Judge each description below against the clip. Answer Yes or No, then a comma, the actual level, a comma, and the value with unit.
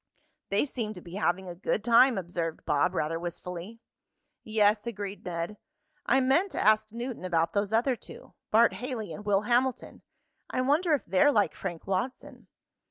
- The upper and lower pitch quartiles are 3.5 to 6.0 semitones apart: Yes, average, 5.1 semitones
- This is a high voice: Yes, high, 210 Hz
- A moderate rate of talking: Yes, average, 165 wpm